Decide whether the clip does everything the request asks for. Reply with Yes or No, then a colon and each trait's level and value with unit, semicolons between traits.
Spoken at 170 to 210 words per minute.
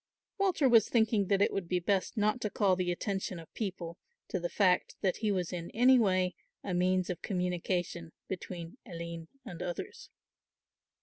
Yes: average, 175 wpm